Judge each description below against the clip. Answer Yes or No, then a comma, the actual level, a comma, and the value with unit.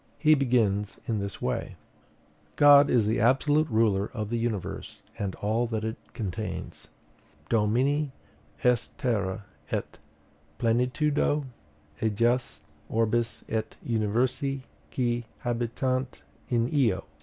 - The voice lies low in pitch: Yes, low, 120 Hz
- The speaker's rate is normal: No, slow, 110 wpm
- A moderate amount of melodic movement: Yes, average, 3.0 semitones